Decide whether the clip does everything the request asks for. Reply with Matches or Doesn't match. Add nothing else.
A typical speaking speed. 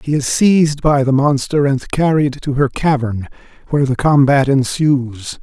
Matches